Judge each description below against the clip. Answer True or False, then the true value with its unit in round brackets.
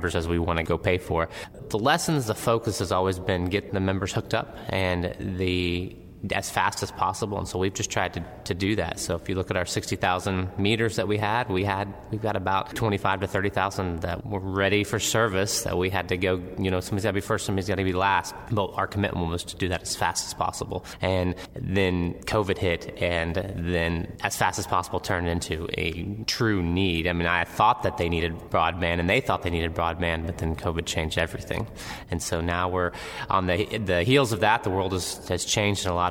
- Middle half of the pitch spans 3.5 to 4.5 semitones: False (2.7 semitones)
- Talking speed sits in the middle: False (230 wpm)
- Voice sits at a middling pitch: False (95 Hz)